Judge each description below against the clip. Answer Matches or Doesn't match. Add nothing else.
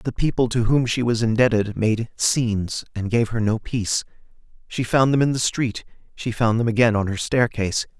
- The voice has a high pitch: Doesn't match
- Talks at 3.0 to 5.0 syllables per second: Doesn't match